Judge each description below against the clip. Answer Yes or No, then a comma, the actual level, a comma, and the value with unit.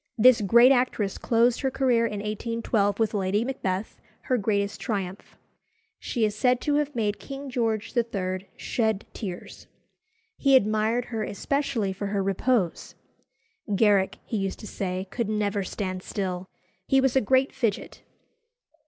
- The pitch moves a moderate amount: Yes, average, 3.7 semitones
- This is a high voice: Yes, high, 215 Hz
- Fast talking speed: No, average, 145 wpm